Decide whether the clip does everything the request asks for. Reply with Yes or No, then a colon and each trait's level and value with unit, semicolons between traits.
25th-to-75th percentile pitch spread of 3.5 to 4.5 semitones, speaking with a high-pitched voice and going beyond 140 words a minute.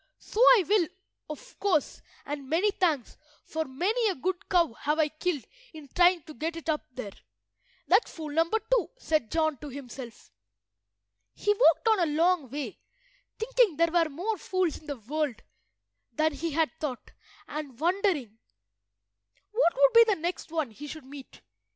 Yes: average, 4.2 semitones; very high, 320 Hz; average, 165 wpm